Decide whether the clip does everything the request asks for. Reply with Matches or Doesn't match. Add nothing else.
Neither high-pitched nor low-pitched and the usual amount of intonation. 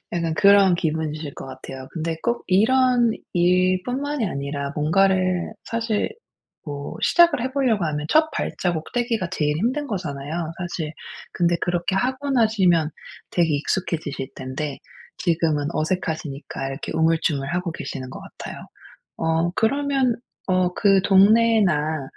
Doesn't match